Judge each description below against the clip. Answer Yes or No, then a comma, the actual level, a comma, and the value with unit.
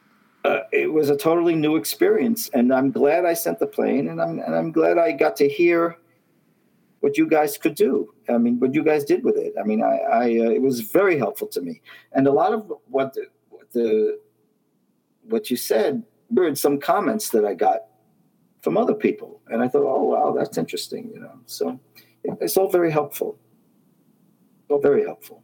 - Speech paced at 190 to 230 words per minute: Yes, average, 200 wpm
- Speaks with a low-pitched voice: No, medium, 180 Hz